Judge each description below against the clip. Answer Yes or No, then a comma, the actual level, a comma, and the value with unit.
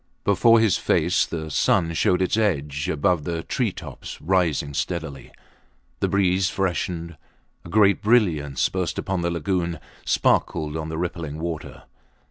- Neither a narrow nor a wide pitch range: Yes, average, 3.3 semitones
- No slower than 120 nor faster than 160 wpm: Yes, average, 140 wpm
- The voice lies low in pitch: Yes, very low, 85 Hz